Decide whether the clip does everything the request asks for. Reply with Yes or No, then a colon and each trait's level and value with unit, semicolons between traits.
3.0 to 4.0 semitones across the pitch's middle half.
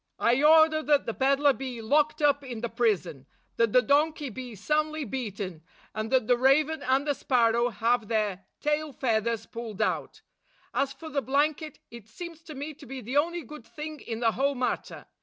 No: average, 4.5 semitones